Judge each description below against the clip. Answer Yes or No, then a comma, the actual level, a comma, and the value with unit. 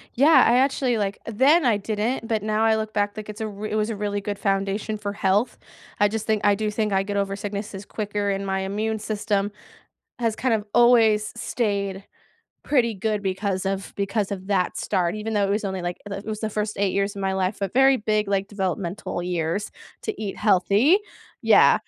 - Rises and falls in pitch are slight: Yes, narrow, 1.7 semitones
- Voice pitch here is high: Yes, high, 205 Hz